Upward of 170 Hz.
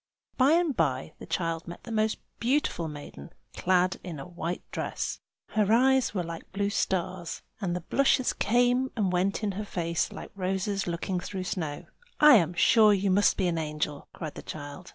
Yes: medium, 185 Hz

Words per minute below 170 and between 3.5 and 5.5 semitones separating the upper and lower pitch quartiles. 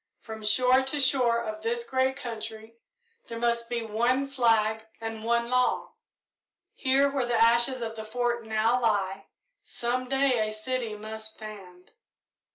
No: average, 150 wpm; narrow, 2.4 semitones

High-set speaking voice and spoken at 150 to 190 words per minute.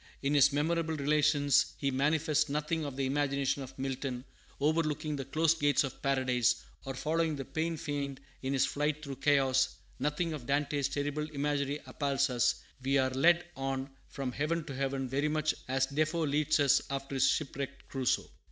No: medium, 140 Hz; average, 170 wpm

